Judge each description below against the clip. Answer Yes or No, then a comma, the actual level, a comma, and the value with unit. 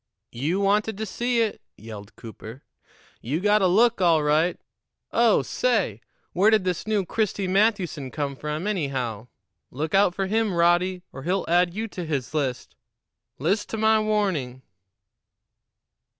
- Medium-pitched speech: Yes, medium, 180 Hz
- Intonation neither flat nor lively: No, wide, 6.0 semitones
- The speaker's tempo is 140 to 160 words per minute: Yes, average, 150 wpm